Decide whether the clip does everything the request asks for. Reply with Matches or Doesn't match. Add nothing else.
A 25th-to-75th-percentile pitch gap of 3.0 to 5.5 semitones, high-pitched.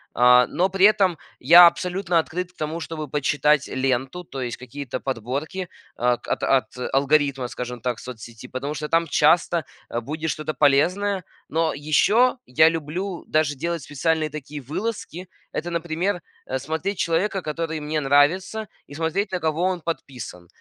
Doesn't match